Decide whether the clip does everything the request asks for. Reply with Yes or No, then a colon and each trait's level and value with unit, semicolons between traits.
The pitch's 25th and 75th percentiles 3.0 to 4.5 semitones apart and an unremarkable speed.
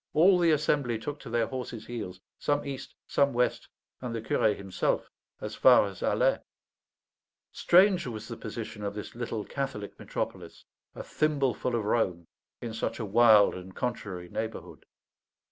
No: average, 4.9 semitones; average, 155 wpm